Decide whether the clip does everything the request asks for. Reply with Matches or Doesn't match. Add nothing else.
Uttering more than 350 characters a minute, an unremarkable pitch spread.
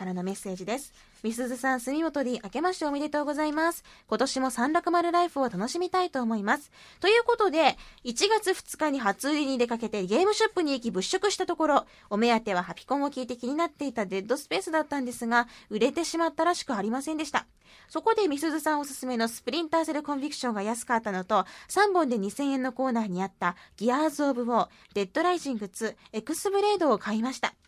Doesn't match